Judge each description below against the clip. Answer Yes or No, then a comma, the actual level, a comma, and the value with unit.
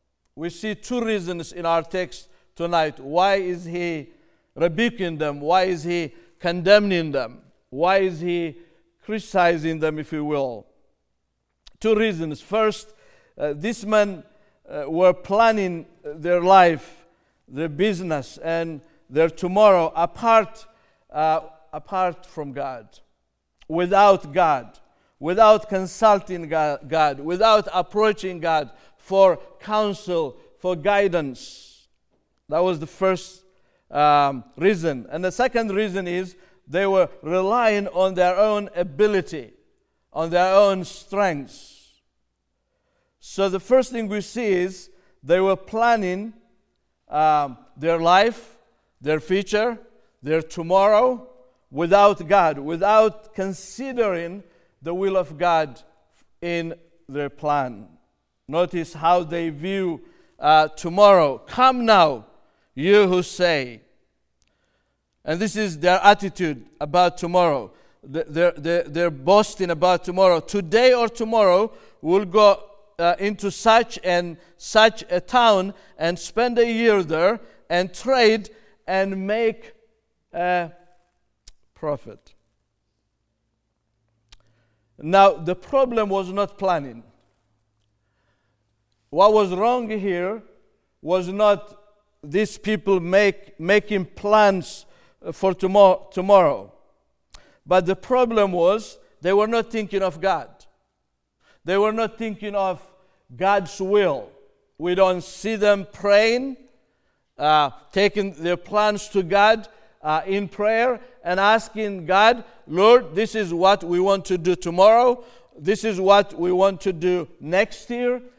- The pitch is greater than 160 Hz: Yes, medium, 185 Hz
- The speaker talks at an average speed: No, slow, 115 wpm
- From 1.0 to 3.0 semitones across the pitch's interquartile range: No, average, 4.2 semitones